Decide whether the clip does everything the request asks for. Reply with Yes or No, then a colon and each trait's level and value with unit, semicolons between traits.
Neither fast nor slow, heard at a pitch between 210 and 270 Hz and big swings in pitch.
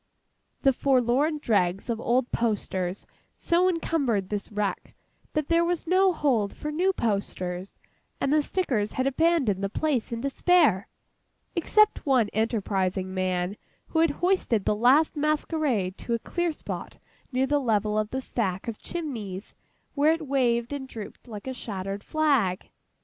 Yes: average, 150 wpm; high, 245 Hz; wide, 6.9 semitones